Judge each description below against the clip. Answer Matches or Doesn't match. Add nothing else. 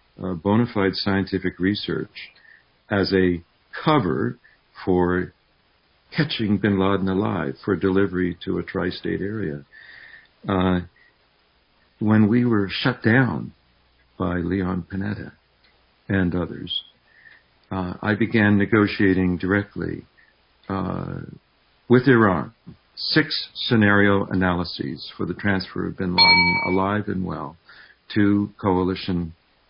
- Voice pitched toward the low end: Matches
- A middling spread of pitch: Doesn't match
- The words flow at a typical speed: Doesn't match